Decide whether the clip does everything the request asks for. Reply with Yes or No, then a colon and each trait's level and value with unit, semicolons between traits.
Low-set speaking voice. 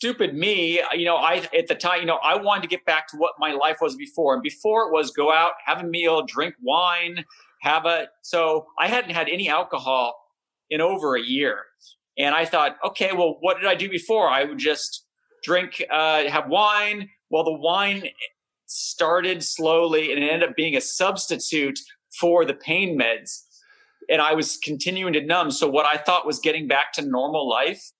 No: medium, 170 Hz